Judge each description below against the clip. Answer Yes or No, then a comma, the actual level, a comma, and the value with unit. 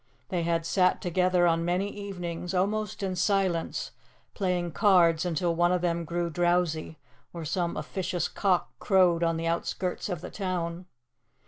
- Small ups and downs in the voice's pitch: Yes, narrow, 1.6 semitones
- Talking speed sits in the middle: Yes, average, 150 wpm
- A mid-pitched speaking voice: Yes, medium, 175 Hz